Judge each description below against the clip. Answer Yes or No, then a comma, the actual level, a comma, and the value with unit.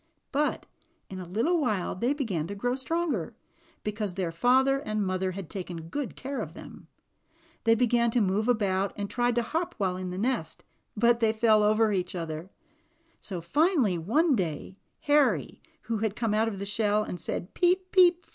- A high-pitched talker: Yes, high, 215 Hz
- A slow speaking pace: No, average, 185 wpm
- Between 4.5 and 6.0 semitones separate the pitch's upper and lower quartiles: Yes, average, 5.2 semitones